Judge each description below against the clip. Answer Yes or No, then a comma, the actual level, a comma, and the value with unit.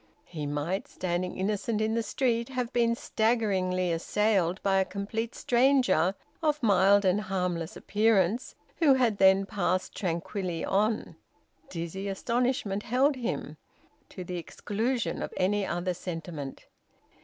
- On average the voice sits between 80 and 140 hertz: No, high, 200 Hz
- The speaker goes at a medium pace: No, slow, 130 wpm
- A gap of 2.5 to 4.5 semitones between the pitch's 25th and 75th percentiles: Yes, average, 4.1 semitones